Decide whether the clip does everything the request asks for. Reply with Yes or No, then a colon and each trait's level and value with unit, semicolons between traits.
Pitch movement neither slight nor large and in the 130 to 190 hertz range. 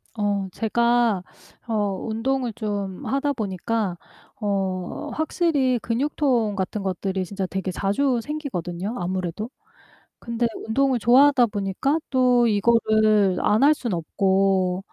No: average, 4.2 semitones; high, 215 Hz